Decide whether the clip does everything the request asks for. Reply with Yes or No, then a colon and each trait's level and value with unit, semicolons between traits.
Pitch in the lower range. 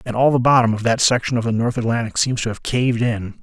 Yes: low, 120 Hz